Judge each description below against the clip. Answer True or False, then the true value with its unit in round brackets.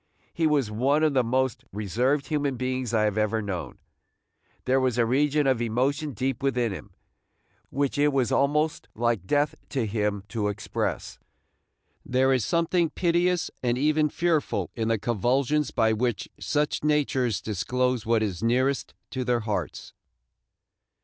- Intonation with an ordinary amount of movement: True (4.3 semitones)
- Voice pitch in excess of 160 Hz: False (130 Hz)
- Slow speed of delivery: False (150 wpm)